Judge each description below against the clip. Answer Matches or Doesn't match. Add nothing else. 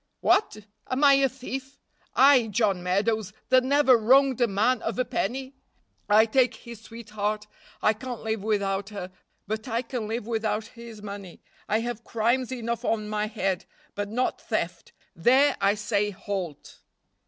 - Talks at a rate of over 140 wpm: Matches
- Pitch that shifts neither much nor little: Matches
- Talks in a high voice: Matches